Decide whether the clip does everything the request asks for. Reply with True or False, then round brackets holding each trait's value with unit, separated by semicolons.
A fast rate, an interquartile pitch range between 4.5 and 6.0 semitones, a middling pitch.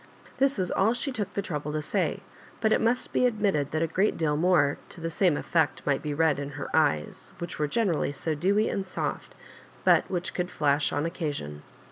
True (210 wpm; 5.0 semitones; 165 Hz)